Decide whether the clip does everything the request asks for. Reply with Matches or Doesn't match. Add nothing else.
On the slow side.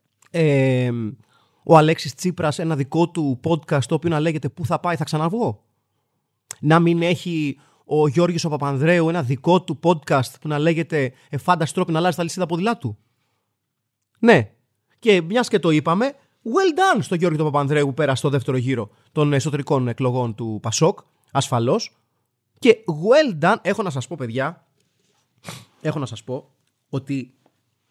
Doesn't match